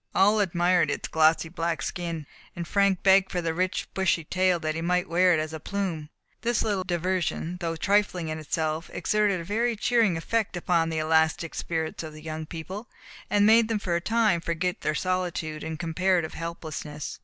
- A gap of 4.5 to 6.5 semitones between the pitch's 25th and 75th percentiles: No, average, 3.1 semitones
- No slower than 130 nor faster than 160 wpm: No, average, 190 wpm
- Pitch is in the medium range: Yes, medium, 175 Hz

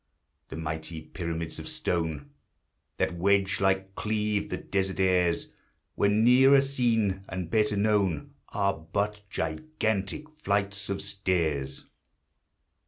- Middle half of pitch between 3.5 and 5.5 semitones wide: Yes, average, 3.8 semitones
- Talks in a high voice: No, very low, 95 Hz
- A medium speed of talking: No, slow, 110 wpm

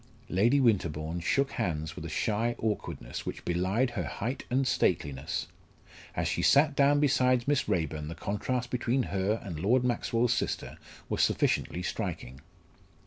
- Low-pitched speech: Yes, low, 110 Hz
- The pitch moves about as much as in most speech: No, wide, 6.6 semitones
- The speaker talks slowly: No, average, 145 wpm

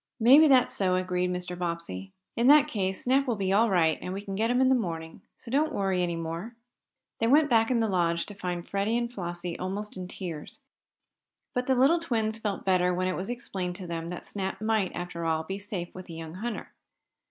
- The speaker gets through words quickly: Yes, fast, 220 wpm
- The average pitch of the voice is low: No, high, 190 Hz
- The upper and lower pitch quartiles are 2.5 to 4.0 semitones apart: No, average, 4.7 semitones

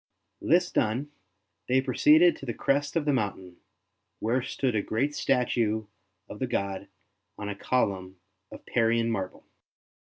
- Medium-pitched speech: No, low, 120 Hz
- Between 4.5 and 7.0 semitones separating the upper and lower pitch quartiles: Yes, average, 4.8 semitones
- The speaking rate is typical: Yes, average, 145 wpm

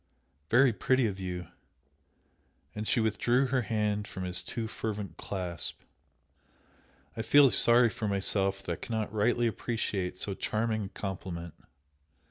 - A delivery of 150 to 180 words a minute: No, slow, 135 wpm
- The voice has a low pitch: Yes, low, 105 Hz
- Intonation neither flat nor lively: Yes, average, 3.4 semitones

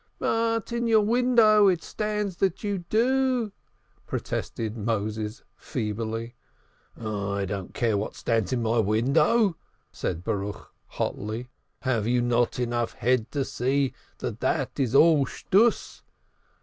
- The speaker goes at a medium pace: No, slow, 125 wpm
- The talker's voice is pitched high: No, low, 125 Hz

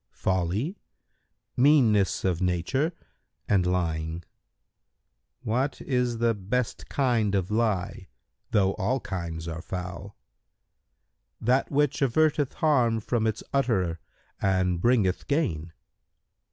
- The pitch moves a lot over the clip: Yes, wide, 5.7 semitones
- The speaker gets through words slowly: Yes, slow, 100 wpm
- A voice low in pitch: Yes, low, 105 Hz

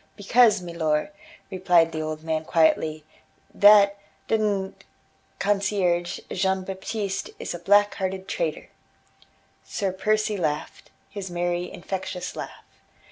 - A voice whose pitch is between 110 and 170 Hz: No, high, 190 Hz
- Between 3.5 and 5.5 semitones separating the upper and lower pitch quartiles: No, average, 2.7 semitones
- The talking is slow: Yes, slow, 115 wpm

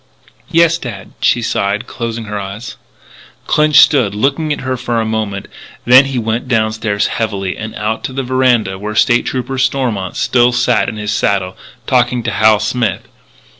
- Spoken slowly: No, average, 165 wpm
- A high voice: No, low, 115 Hz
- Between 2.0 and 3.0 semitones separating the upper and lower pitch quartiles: No, average, 3.4 semitones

